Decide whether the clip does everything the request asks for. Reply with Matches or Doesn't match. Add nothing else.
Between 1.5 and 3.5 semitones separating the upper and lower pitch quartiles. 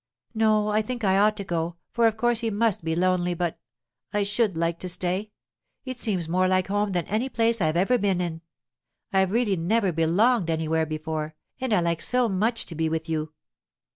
Doesn't match